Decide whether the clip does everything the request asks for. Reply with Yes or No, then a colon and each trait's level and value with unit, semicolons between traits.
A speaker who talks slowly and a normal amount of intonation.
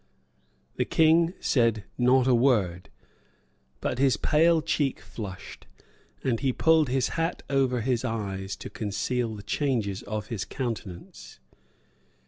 Yes: slow, 125 wpm; average, 4.6 semitones